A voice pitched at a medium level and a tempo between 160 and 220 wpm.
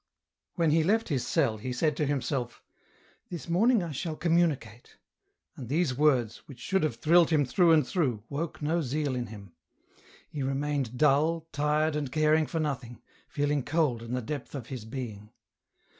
Yes: medium, 145 Hz; average, 175 wpm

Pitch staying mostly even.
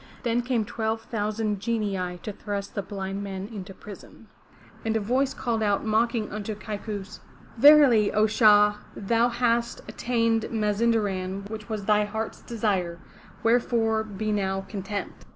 Yes: narrow, 2.1 semitones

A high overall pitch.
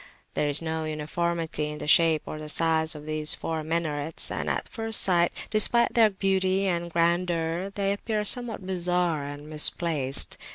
No: medium, 170 Hz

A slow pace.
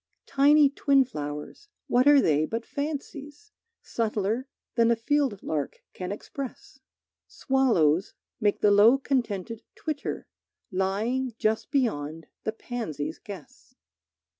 Yes: slow, 115 wpm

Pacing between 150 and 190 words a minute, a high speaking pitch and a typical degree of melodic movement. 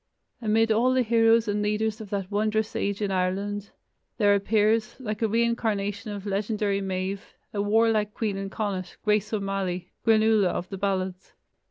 No: average, 160 wpm; high, 210 Hz; narrow, 1.9 semitones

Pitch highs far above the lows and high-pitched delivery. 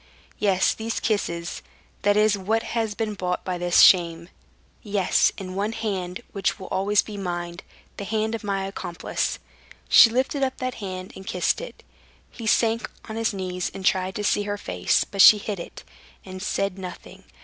No: average, 2.8 semitones; high, 195 Hz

